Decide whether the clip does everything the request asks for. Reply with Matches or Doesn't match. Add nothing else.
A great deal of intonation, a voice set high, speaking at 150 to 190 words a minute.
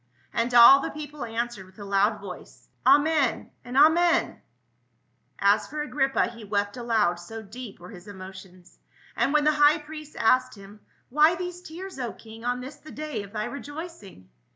Matches